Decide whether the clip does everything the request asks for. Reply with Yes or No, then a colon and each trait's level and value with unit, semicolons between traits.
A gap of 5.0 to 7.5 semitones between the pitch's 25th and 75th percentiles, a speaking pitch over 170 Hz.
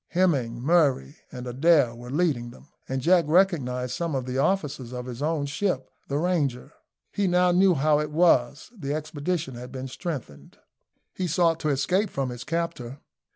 No: average, 5.3 semitones; medium, 145 Hz